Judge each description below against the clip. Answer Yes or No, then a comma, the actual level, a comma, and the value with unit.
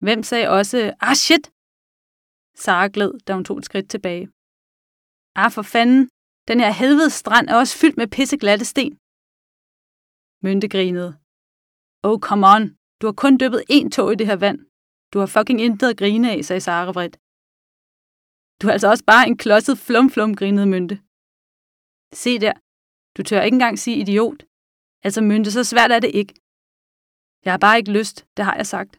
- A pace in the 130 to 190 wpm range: Yes, average, 180 wpm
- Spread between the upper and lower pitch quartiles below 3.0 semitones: No, average, 3.4 semitones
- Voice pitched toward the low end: No, high, 215 Hz